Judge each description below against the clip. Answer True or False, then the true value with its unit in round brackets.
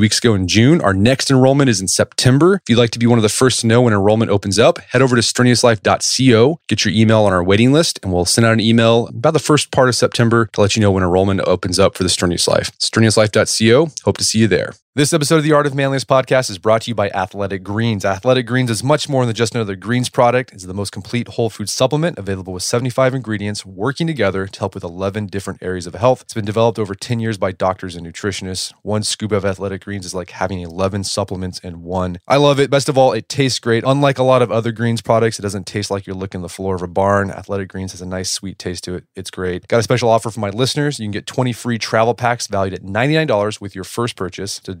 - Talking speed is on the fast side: True (260 wpm)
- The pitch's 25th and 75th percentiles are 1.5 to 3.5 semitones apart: False (4.1 semitones)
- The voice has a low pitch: True (110 Hz)